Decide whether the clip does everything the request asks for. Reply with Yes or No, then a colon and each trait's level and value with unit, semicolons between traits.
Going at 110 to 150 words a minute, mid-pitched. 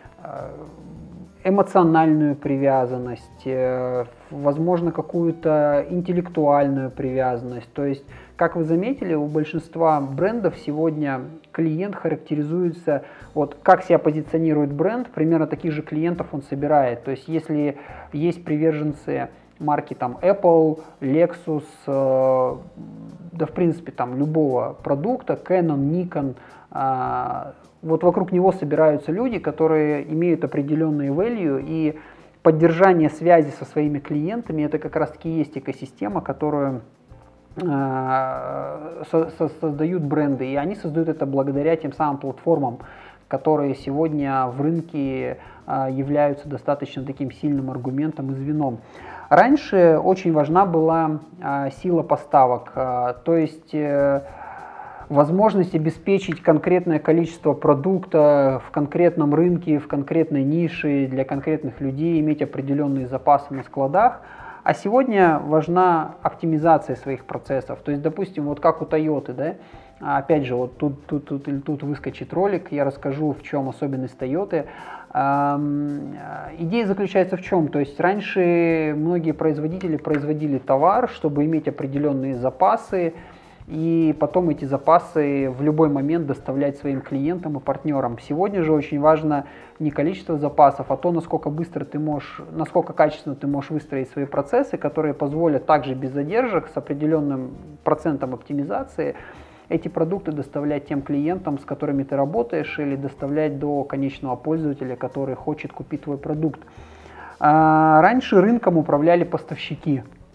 Yes: average, 125 wpm; medium, 150 Hz